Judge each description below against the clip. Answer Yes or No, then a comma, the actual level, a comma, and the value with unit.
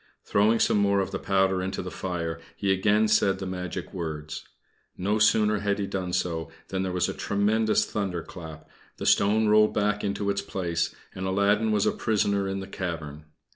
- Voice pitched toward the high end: No, very low, 95 Hz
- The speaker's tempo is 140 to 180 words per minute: No, average, 190 wpm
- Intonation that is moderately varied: No, narrow, 2.3 semitones